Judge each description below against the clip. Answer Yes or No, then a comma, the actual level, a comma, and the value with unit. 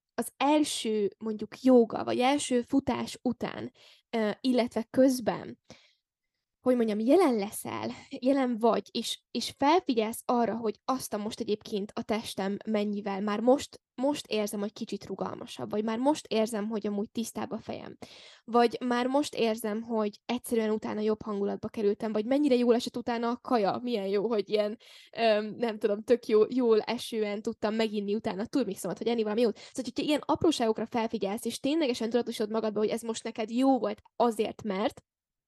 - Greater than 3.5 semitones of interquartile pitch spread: No, narrow, 2.5 semitones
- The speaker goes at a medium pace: No, fast, 165 wpm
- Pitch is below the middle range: No, high, 225 Hz